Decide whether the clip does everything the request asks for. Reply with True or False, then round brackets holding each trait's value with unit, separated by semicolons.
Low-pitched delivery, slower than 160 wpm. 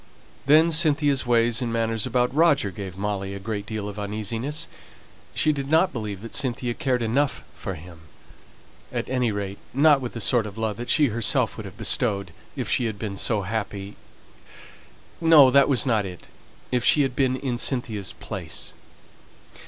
False (115 Hz; 175 wpm)